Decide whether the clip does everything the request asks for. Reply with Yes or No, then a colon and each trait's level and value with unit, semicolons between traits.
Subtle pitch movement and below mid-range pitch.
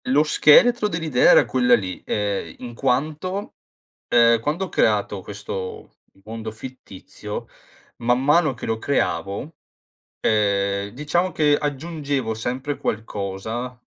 No: wide, 5.8 semitones; low, 125 Hz